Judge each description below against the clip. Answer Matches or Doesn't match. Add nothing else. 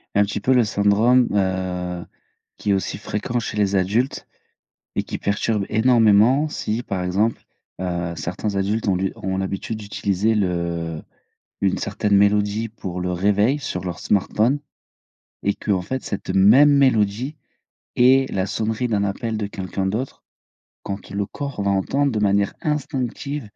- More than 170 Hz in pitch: Doesn't match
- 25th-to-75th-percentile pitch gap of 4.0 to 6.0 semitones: Doesn't match